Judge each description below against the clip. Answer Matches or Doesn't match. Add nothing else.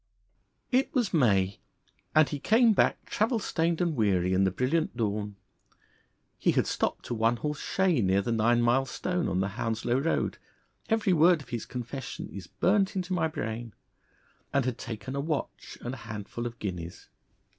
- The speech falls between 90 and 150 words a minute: Doesn't match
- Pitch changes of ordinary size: Doesn't match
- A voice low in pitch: Matches